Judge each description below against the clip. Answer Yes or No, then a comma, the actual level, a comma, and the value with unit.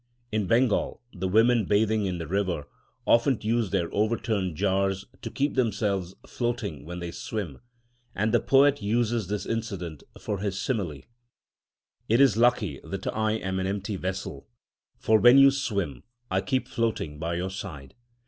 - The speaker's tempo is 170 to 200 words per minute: No, average, 160 wpm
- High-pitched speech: No, low, 100 Hz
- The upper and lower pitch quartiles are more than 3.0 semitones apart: Yes, average, 3.8 semitones